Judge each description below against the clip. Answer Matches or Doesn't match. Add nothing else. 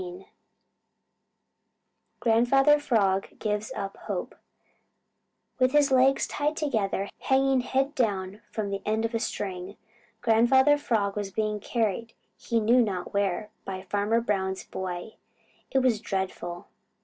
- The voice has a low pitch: Doesn't match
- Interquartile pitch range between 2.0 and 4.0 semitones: Doesn't match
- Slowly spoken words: Matches